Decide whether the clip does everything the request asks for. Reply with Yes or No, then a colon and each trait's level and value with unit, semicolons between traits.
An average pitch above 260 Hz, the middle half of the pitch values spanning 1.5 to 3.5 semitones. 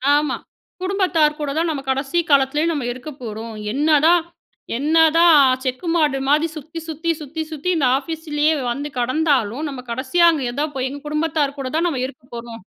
Yes: very high, 295 Hz; average, 3.2 semitones